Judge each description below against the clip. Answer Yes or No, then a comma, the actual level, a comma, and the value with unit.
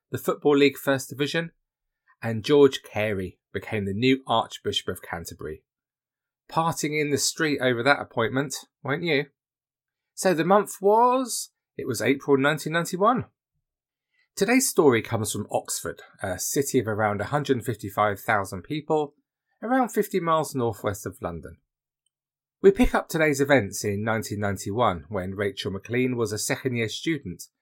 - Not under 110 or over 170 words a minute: Yes, average, 155 wpm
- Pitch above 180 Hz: No, low, 135 Hz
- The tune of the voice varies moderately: No, wide, 6.5 semitones